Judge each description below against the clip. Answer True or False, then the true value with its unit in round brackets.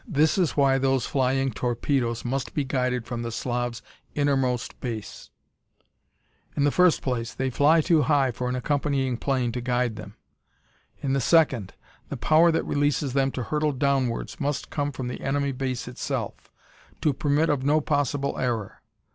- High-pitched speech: False (135 Hz)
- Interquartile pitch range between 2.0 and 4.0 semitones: True (2.7 semitones)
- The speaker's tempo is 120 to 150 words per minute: False (165 wpm)